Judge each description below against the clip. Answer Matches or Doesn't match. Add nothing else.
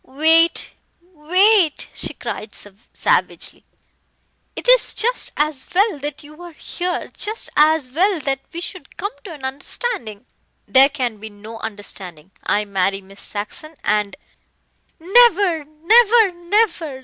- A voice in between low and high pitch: Doesn't match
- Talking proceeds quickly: Doesn't match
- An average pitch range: Doesn't match